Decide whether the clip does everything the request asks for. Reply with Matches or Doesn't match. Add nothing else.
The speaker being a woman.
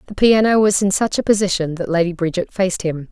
Matches